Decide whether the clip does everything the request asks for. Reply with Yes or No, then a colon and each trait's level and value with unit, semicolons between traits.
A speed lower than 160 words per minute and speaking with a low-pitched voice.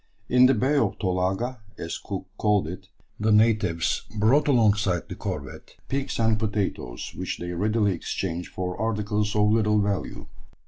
Yes: average, 150 wpm; low, 105 Hz